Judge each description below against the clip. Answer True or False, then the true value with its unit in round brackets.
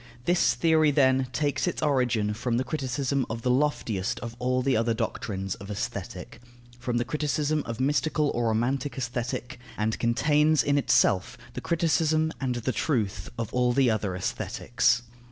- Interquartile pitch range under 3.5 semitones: False (4.0 semitones)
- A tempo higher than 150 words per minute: True (160 wpm)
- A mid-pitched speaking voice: False (125 Hz)